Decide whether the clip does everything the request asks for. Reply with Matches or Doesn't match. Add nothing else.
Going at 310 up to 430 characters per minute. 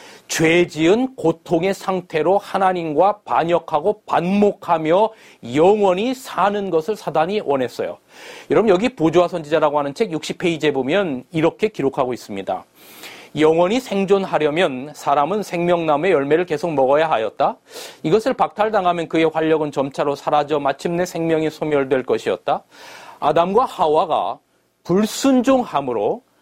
Matches